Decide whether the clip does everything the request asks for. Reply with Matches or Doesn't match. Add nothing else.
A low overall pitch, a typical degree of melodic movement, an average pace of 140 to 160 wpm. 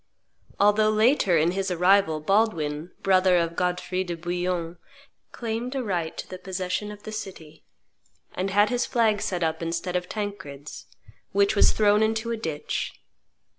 Doesn't match